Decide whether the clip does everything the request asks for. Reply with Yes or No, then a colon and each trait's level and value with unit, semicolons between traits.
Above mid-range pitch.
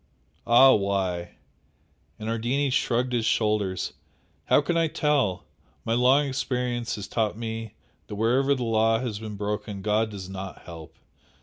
No: low, 115 Hz